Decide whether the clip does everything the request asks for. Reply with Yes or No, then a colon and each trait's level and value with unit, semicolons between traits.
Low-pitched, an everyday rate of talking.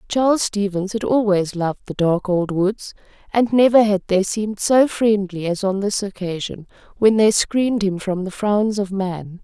No: high, 200 Hz; average, 185 wpm